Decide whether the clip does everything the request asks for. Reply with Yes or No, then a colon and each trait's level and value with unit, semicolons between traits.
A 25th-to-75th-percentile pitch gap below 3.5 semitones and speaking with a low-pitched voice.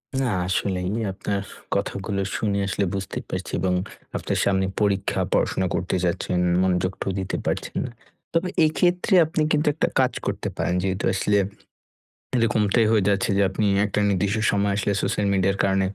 Yes: narrow, 2.5 semitones; low, 100 Hz